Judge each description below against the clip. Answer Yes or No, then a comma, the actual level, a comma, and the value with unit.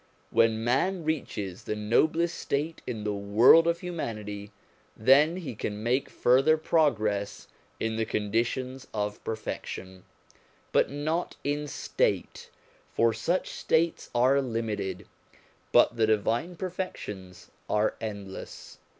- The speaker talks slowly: Yes, slow, 115 wpm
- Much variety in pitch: Yes, wide, 6.6 semitones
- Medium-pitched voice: No, low, 115 Hz